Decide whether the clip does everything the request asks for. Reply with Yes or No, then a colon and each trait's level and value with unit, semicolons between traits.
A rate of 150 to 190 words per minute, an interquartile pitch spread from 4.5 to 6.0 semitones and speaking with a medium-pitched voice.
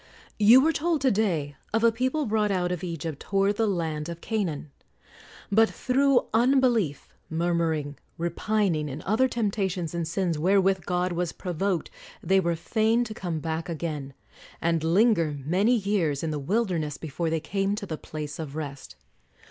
Yes: average, 165 wpm; average, 5.2 semitones; medium, 180 Hz